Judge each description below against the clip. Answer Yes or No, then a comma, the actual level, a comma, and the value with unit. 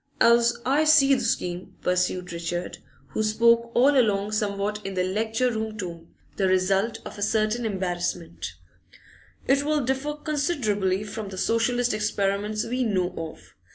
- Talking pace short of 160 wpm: Yes, average, 150 wpm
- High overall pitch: Yes, high, 215 Hz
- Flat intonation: No, average, 4.2 semitones